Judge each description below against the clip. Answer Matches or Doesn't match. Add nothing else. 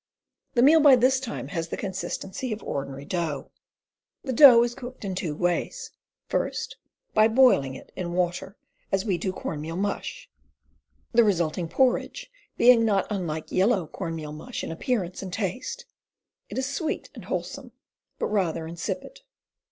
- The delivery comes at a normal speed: Matches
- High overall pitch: Matches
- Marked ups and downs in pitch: Matches